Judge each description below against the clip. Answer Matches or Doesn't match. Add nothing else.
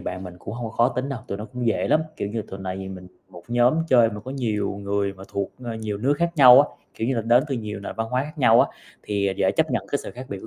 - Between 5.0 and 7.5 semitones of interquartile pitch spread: Doesn't match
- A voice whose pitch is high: Doesn't match